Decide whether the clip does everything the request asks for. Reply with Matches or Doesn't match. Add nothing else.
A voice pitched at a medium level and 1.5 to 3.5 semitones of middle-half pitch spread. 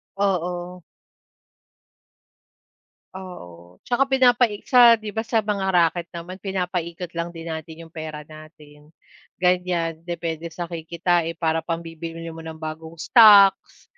Matches